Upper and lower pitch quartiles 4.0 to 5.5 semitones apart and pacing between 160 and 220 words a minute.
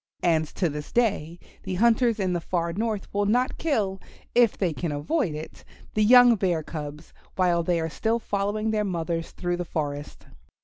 Yes: average, 4.7 semitones; average, 180 wpm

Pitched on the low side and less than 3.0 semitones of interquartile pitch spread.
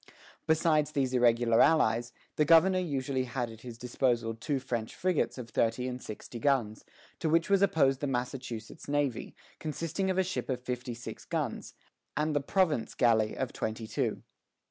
No: low, 130 Hz; average, 4.5 semitones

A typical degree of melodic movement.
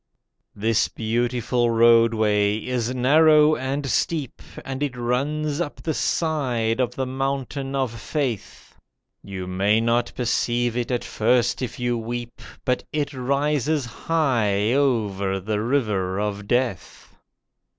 Yes: average, 3.5 semitones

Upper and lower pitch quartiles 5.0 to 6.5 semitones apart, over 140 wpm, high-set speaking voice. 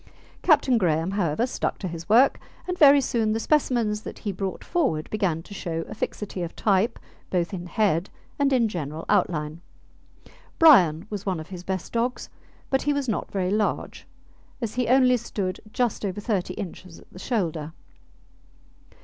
Yes: wide, 5.5 semitones; average, 170 wpm; high, 200 Hz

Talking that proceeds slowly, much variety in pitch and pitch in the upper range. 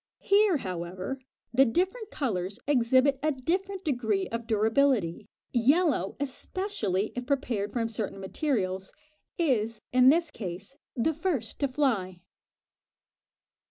Yes: slow, 115 wpm; wide, 6.3 semitones; very high, 250 Hz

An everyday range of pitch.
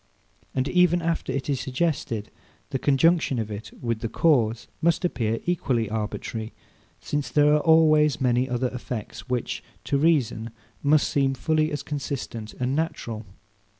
Yes: average, 4.7 semitones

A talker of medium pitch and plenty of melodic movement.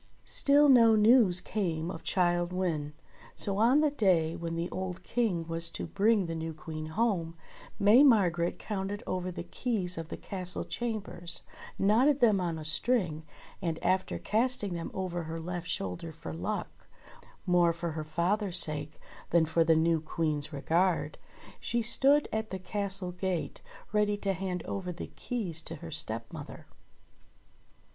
No: medium, 180 Hz; average, 4.1 semitones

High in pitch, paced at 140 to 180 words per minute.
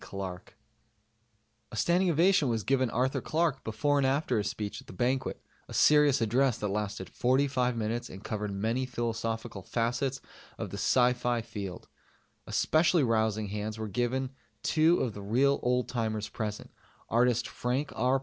No: low, 120 Hz; average, 160 wpm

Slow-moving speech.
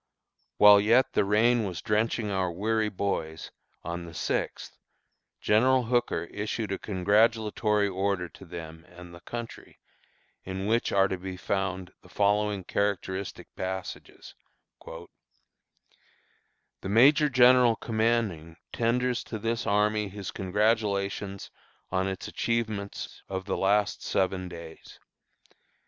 Yes: slow, 120 wpm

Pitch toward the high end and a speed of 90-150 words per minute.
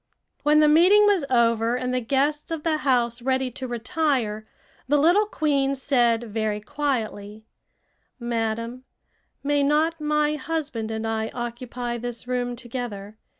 Yes: very high, 250 Hz; average, 140 wpm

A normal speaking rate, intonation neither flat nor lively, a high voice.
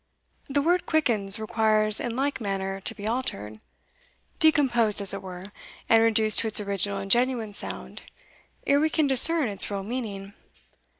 Yes: average, 160 wpm; average, 4.6 semitones; high, 220 Hz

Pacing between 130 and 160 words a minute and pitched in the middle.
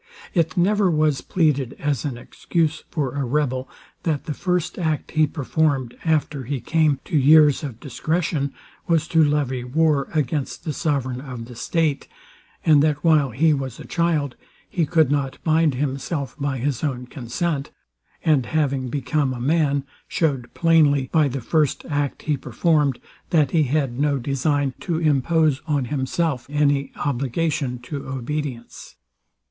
Yes: average, 155 wpm; medium, 145 Hz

